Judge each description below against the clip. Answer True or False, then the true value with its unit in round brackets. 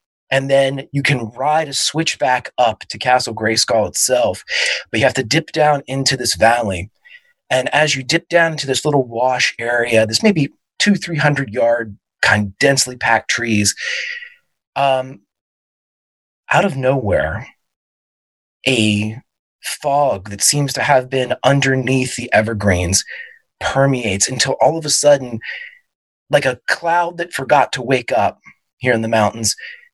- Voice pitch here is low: True (130 Hz)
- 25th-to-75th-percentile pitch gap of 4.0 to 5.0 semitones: True (4.7 semitones)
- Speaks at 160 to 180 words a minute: False (150 wpm)